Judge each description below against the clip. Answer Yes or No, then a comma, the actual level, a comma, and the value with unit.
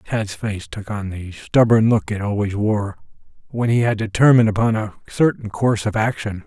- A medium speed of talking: Yes, average, 185 wpm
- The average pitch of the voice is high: No, low, 105 Hz